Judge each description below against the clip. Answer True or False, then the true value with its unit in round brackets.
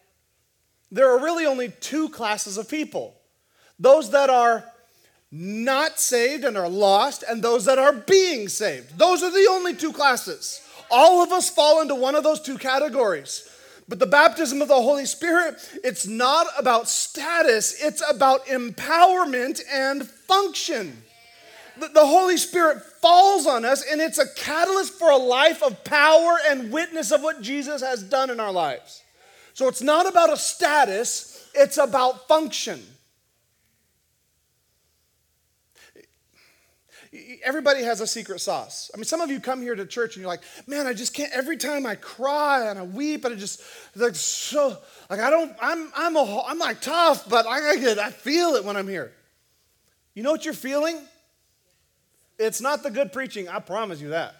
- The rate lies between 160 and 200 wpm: True (170 wpm)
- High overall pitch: True (280 Hz)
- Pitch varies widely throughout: False (5.0 semitones)